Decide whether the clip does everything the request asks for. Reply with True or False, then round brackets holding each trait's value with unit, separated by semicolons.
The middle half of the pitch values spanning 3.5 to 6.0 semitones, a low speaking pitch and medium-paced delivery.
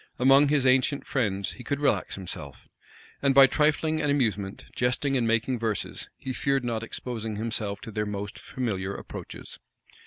True (4.3 semitones; 125 Hz; 160 wpm)